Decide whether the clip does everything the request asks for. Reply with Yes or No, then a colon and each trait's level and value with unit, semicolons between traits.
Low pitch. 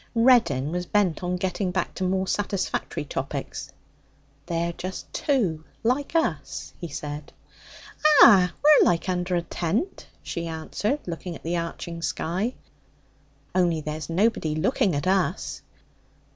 No: medium, 180 Hz